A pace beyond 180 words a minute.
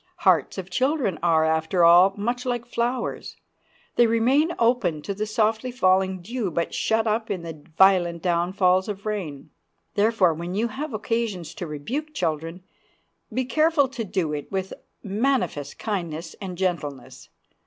No: average, 150 wpm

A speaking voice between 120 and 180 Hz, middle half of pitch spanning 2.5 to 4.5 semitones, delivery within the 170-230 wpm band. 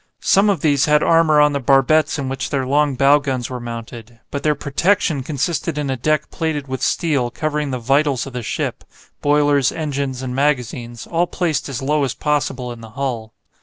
Yes: medium, 140 Hz; average, 2.8 semitones; average, 200 wpm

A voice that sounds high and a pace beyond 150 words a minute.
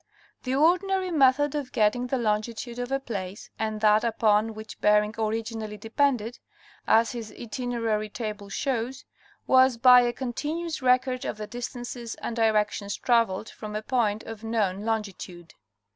No: high, 230 Hz; average, 145 wpm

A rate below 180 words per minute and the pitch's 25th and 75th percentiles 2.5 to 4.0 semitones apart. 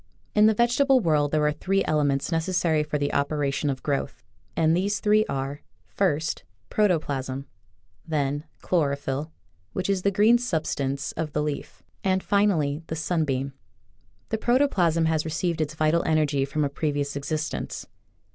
No: average, 155 wpm; average, 4.5 semitones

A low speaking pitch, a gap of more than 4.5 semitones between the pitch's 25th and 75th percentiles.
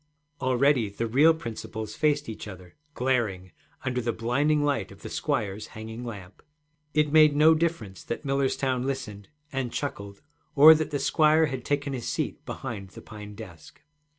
Yes: low, 125 Hz; average, 5.3 semitones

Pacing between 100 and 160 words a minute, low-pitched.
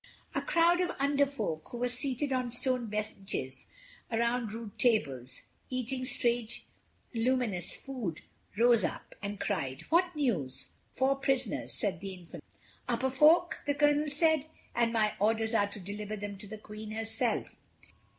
No: average, 150 wpm; high, 235 Hz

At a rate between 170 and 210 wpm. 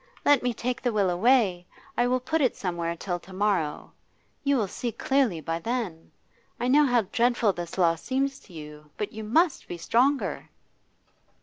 Yes: average, 180 wpm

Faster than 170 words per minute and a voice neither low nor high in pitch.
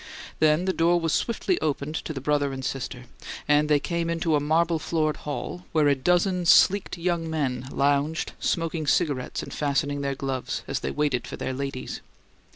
Yes: average, 180 wpm; medium, 150 Hz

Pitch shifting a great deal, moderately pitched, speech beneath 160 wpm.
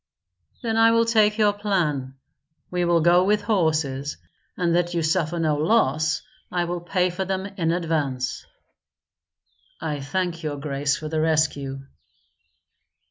No: average, 3.7 semitones; medium, 170 Hz; average, 140 wpm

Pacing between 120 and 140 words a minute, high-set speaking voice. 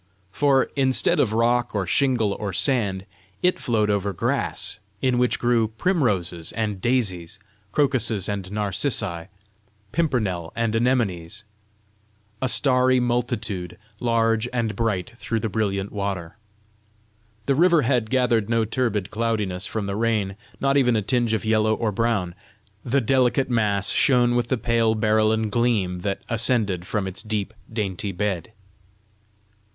No: slow, 135 wpm; low, 110 Hz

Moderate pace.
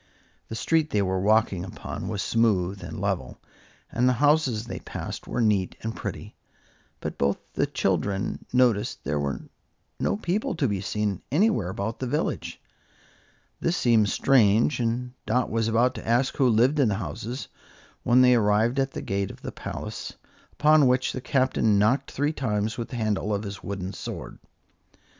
Yes: average, 170 wpm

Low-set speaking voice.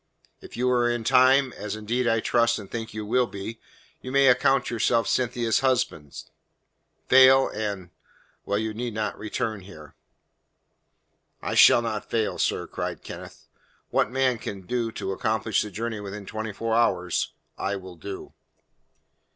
Yes: low, 110 Hz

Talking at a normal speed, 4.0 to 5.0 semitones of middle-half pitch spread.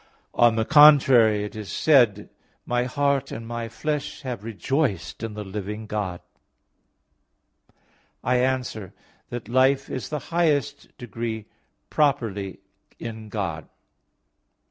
No: slow, 125 wpm; average, 4.3 semitones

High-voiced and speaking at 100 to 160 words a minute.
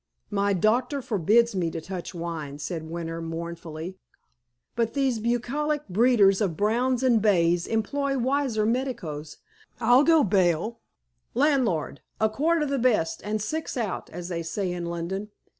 Yes: high, 210 Hz; average, 145 wpm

